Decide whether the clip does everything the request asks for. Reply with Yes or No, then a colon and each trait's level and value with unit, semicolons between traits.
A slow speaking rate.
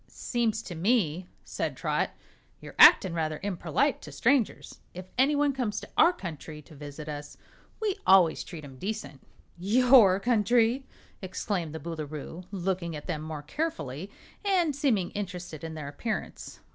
No: average, 145 wpm